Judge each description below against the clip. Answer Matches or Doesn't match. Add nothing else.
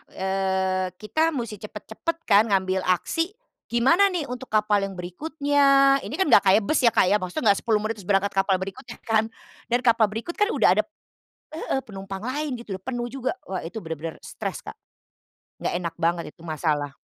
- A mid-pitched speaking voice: Doesn't match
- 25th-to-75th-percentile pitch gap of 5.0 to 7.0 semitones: Matches